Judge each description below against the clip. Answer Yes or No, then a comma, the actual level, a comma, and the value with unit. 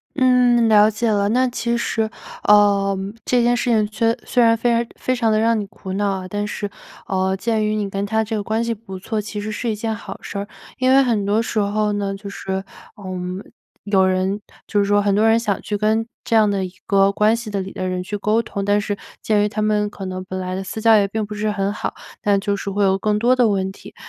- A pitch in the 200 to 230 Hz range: Yes, high, 210 Hz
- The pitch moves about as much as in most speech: No, narrow, 2.0 semitones